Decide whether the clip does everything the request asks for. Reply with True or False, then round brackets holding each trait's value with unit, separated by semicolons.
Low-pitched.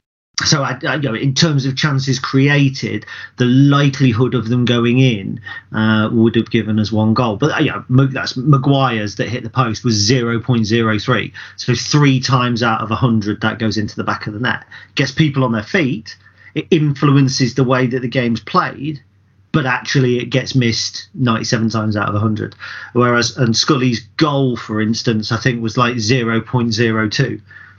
True (125 Hz)